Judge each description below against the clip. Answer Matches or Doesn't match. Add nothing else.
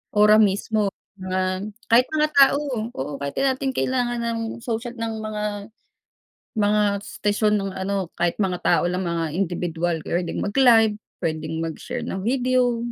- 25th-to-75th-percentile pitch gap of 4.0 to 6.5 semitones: Matches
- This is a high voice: Matches